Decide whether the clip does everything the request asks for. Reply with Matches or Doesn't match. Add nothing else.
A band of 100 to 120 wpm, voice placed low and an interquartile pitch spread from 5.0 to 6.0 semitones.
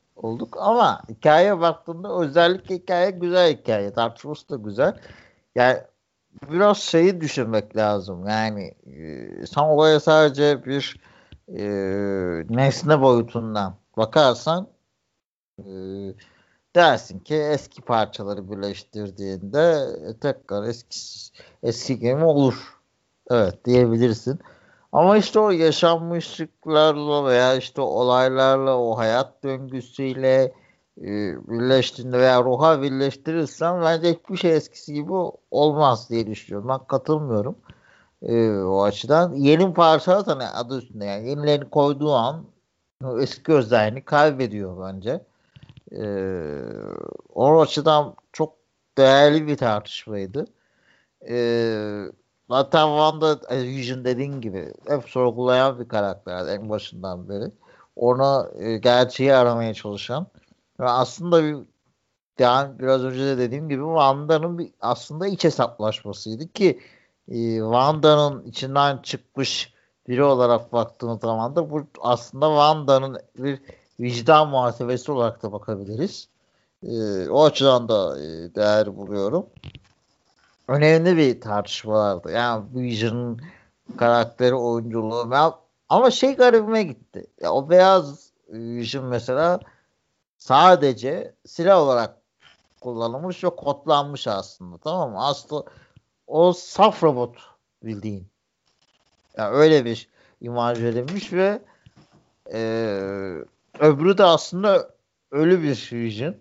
Matches